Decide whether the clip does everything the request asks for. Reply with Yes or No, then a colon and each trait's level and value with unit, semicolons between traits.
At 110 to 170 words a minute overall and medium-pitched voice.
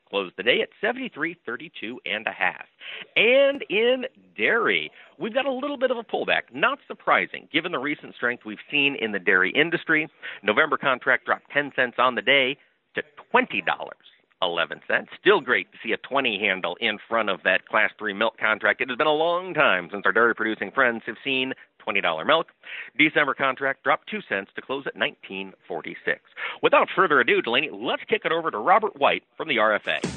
No: average, 190 wpm; medium, 150 Hz